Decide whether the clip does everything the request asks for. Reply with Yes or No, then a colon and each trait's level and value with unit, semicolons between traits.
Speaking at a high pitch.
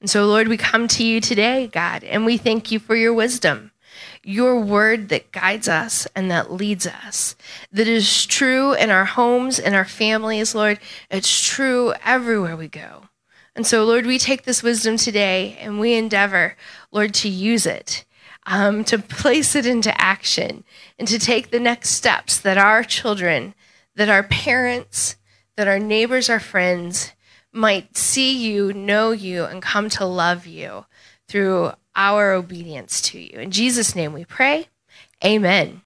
Yes: high, 215 Hz